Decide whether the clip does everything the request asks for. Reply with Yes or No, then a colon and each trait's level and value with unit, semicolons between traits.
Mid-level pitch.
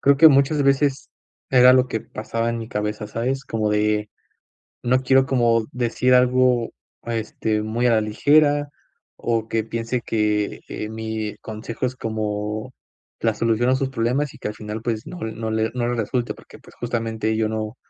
No: low, 115 Hz